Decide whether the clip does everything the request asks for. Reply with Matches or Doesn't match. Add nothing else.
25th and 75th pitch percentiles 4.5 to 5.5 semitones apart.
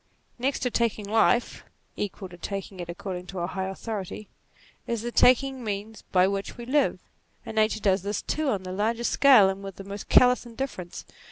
Doesn't match